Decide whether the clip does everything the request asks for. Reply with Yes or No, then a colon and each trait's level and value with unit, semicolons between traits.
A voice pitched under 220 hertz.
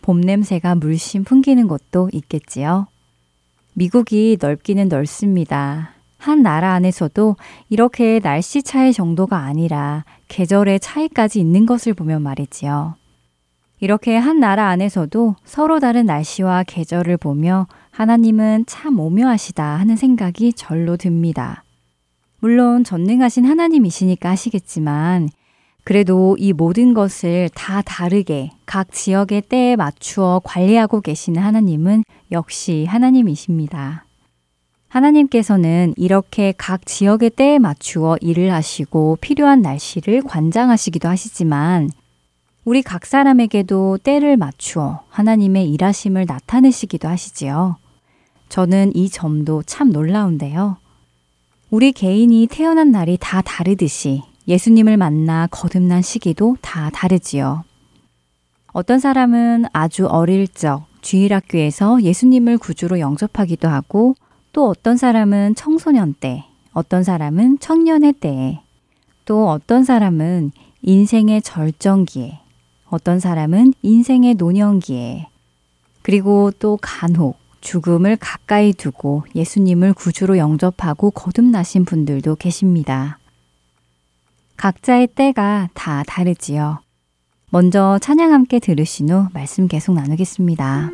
Yes: medium, 185 Hz